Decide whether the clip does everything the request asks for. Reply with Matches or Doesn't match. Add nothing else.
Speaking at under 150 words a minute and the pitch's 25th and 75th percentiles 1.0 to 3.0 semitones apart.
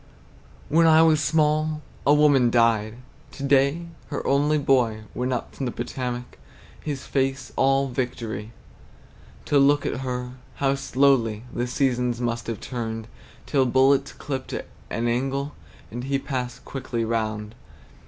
Matches